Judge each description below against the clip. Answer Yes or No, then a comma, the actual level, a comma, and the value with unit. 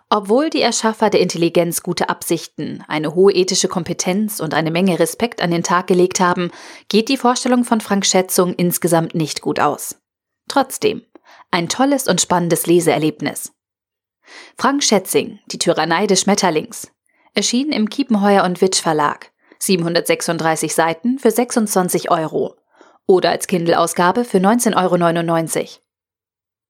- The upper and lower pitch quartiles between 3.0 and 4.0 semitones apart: No, average, 4.4 semitones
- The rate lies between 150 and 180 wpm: No, average, 135 wpm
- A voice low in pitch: No, medium, 185 Hz